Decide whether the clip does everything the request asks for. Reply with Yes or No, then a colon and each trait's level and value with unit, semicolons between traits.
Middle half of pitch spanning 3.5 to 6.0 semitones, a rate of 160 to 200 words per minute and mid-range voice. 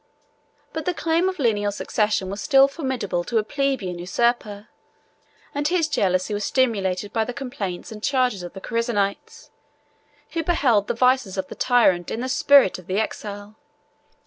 No: average, 5.1 semitones; average, 165 wpm; high, 225 Hz